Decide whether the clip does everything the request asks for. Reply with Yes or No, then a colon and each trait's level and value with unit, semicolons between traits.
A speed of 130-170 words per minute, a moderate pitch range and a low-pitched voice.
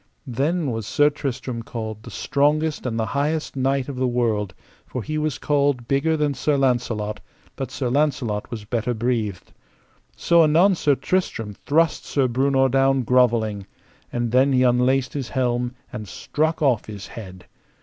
Yes: average, 160 wpm; average, 3.7 semitones; low, 130 Hz